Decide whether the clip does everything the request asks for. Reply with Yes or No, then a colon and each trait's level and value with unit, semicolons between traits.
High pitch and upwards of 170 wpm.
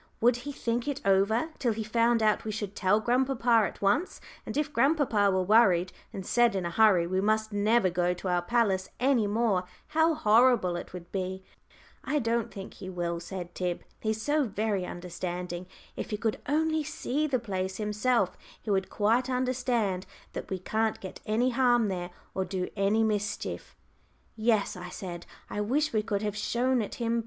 Yes: high, 215 Hz; average, 185 wpm